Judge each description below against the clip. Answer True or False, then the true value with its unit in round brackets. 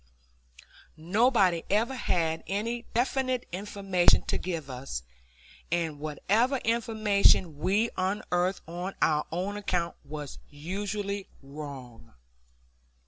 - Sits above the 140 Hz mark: True (185 Hz)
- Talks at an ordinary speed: False (95 wpm)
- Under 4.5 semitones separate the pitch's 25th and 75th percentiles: False (4.9 semitones)